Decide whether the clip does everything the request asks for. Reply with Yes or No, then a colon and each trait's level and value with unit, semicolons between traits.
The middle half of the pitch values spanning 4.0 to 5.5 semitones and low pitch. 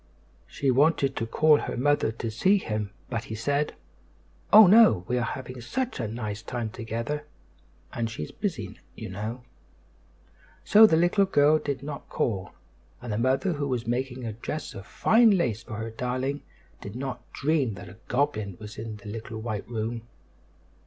Yes: average, 4.7 semitones; low, 125 Hz